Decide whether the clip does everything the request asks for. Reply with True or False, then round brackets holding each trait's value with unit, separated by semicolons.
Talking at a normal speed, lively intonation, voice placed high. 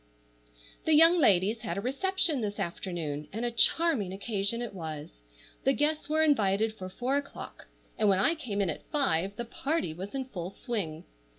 True (180 wpm; 6.8 semitones; 215 Hz)